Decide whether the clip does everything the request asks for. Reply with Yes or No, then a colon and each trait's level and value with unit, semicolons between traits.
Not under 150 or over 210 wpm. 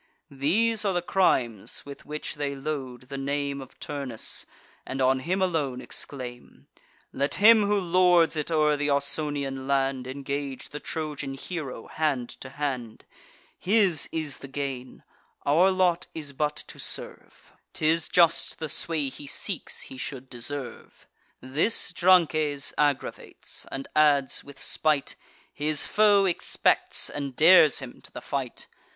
No: average, 140 wpm